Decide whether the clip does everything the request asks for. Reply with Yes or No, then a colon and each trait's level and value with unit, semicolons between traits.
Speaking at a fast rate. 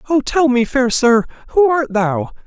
No: average, 195 wpm